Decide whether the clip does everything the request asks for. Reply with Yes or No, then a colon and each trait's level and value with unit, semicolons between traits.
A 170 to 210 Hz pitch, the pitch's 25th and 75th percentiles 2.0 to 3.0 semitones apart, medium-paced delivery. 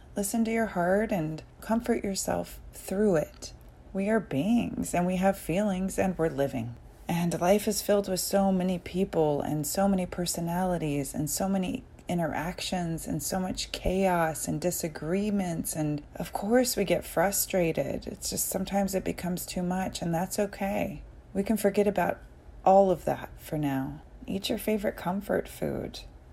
No: medium, 185 Hz; average, 4.1 semitones; average, 160 wpm